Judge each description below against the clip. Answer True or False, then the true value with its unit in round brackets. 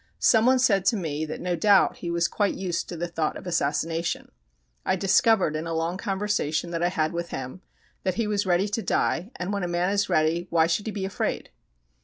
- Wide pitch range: False (3.3 semitones)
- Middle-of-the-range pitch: True (175 Hz)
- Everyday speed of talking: False (220 wpm)